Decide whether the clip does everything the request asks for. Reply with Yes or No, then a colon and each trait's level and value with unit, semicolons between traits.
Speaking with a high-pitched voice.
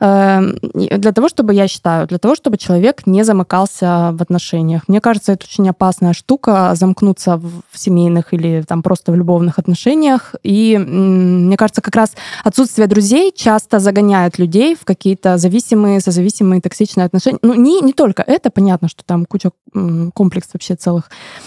Yes: high, 195 Hz